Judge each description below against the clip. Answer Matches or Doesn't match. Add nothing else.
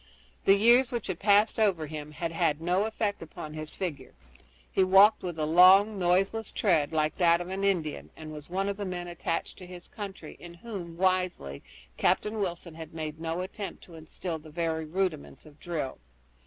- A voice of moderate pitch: Matches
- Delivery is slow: Doesn't match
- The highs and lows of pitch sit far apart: Doesn't match